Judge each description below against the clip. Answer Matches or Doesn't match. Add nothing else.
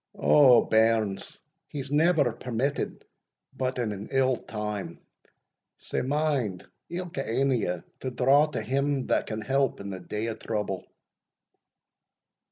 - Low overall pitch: Matches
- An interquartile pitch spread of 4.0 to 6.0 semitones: Matches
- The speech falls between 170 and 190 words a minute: Doesn't match